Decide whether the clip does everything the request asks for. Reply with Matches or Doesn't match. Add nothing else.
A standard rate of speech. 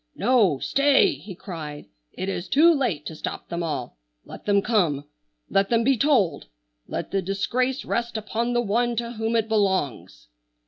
Matches